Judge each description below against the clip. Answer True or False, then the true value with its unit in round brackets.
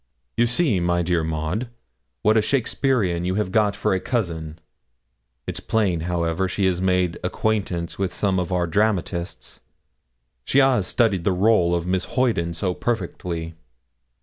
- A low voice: True (95 Hz)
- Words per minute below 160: True (150 wpm)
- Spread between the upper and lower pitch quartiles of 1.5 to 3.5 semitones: False (4.0 semitones)